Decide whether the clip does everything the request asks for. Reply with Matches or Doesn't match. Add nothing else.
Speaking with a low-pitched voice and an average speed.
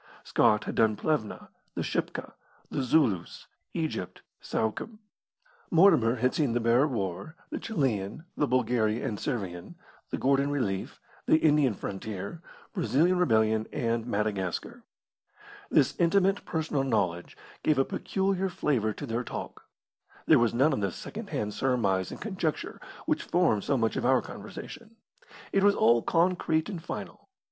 Matches